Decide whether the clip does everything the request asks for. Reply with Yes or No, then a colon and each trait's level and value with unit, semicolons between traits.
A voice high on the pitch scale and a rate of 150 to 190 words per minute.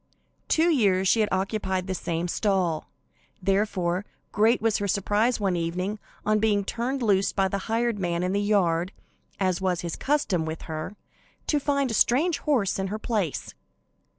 Yes: high, 200 Hz; average, 170 wpm